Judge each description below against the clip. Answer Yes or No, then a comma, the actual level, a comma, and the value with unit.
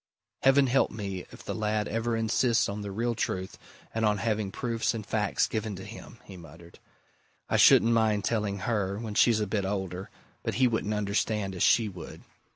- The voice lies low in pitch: Yes, low, 105 Hz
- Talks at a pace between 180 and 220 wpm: Yes, average, 190 wpm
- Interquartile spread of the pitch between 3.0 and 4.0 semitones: No, narrow, 2.5 semitones